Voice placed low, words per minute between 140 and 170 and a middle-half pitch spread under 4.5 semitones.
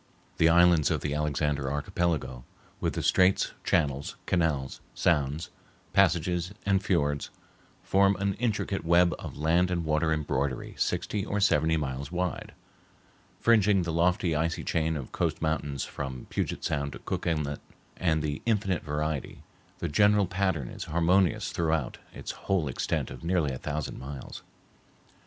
Yes: very low, 80 Hz; average, 145 wpm; average, 3.9 semitones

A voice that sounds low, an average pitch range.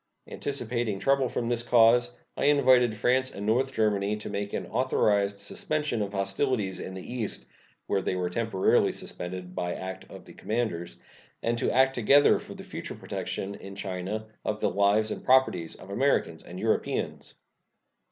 Yes: low, 110 Hz; average, 3.9 semitones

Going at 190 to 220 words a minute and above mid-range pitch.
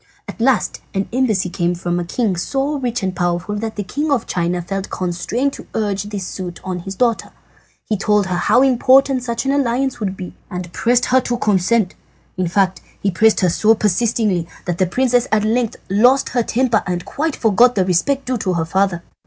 Yes: average, 200 wpm; high, 210 Hz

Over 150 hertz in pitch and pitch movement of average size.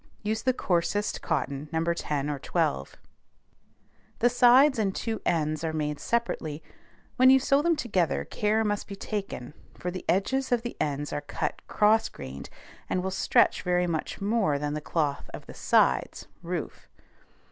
No: medium, 185 Hz; wide, 6.8 semitones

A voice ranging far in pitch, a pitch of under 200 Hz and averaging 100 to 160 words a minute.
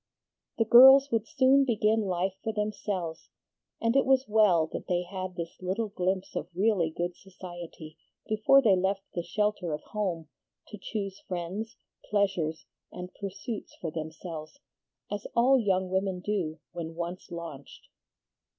No: average, 3.6 semitones; high, 190 Hz; average, 145 wpm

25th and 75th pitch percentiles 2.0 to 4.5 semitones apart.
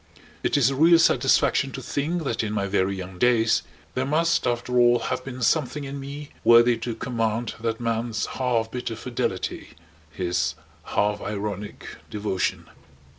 Yes: average, 3.4 semitones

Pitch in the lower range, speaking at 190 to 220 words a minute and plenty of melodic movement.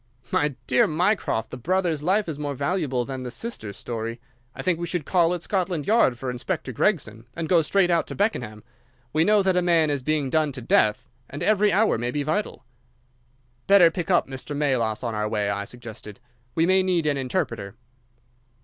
No: medium, 150 Hz; average, 195 wpm; wide, 6.6 semitones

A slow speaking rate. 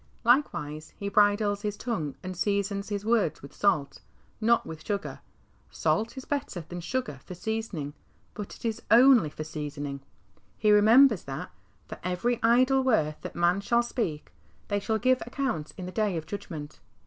No: average, 170 wpm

